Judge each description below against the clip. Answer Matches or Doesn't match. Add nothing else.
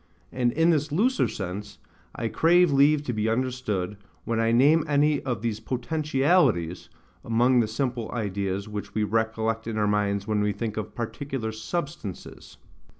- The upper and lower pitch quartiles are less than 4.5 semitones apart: Doesn't match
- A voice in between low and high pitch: Doesn't match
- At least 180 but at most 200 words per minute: Doesn't match